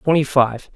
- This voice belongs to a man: Yes, male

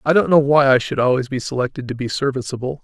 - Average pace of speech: No, fast, 255 wpm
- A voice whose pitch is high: No, low, 135 Hz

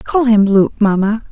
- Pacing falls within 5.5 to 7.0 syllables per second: No, 4.2 syllables/s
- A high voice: Yes, high, 215 Hz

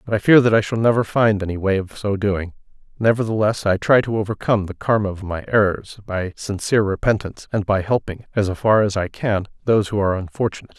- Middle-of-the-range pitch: No, low, 105 Hz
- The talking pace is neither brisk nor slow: No, fast, 210 wpm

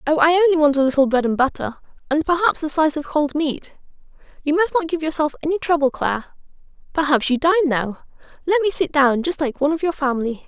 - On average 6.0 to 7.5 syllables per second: Yes, 6.3 syllables/s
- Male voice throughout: No, female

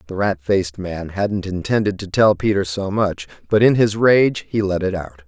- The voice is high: No, very low, 95 Hz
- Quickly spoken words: Yes, fast, 215 wpm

